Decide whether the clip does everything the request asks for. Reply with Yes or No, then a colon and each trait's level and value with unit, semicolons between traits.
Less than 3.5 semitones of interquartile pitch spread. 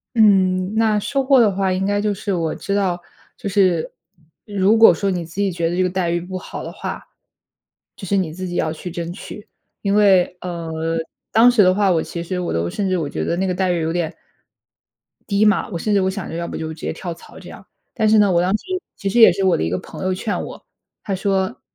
Yes: average, 2.8 semitones